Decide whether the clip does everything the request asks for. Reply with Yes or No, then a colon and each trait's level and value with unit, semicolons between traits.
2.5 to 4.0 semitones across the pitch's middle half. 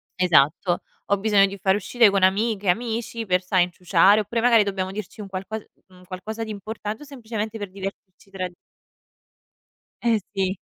Yes: average, 2.8 semitones